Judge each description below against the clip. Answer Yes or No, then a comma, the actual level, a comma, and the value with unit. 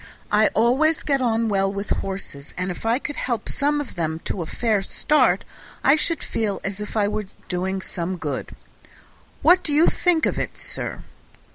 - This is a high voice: Yes, high, 215 Hz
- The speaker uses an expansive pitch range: Yes, wide, 6.8 semitones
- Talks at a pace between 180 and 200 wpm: Yes, average, 185 wpm